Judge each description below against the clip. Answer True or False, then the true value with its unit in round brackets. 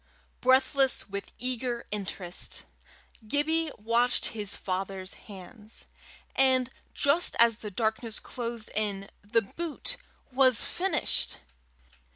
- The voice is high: True (230 Hz)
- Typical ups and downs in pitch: True (4.4 semitones)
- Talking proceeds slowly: True (100 wpm)